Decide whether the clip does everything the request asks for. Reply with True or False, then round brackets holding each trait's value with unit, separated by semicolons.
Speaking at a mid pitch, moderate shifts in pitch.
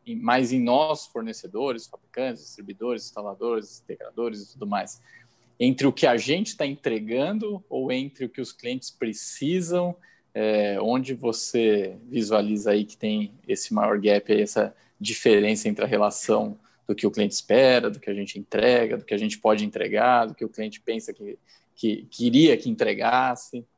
False (115 Hz; 3.9 semitones)